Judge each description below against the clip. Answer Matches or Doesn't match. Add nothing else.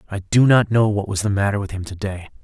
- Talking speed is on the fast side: Matches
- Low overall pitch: Matches